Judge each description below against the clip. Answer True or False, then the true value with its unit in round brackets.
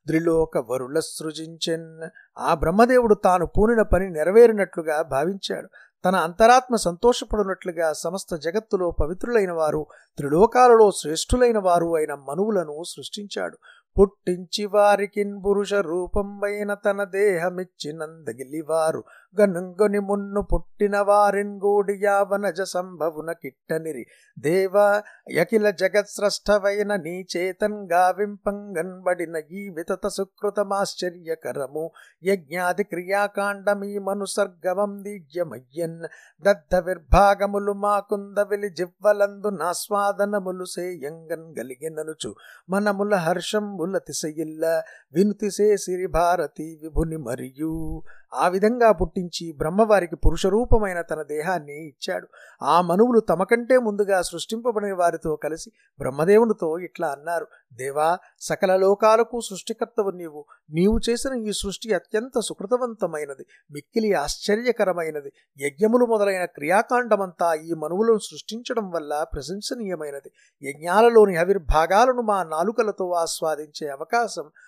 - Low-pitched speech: False (190 Hz)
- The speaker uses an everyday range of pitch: True (4.0 semitones)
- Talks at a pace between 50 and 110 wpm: True (90 wpm)